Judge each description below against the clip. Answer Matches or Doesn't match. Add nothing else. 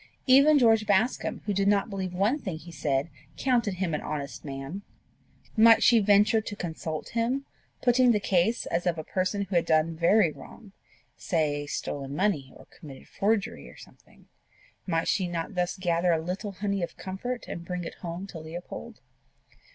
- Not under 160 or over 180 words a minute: Matches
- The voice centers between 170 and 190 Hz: Matches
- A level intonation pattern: Doesn't match